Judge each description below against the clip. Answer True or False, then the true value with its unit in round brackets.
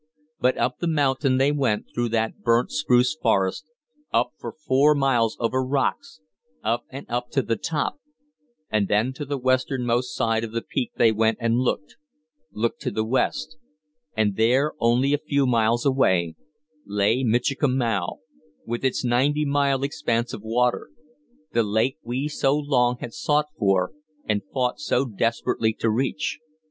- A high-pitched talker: False (125 Hz)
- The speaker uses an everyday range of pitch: True (3.3 semitones)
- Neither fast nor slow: True (155 wpm)